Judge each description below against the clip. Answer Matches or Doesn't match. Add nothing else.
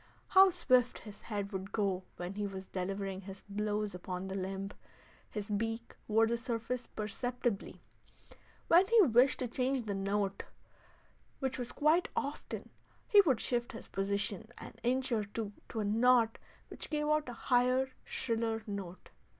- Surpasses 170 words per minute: Doesn't match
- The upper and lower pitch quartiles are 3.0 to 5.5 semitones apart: Matches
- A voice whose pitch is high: Matches